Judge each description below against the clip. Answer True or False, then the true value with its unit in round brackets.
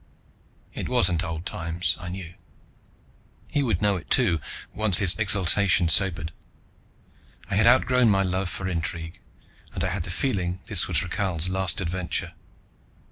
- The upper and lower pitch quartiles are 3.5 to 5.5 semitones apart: False (2.5 semitones)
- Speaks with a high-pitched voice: False (90 Hz)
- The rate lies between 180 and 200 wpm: False (145 wpm)